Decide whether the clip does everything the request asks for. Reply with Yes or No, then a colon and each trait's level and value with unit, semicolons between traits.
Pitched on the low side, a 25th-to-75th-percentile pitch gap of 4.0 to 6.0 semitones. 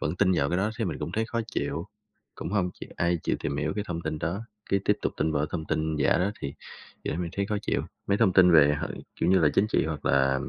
Yes: very low, 85 Hz; average, 4.3 semitones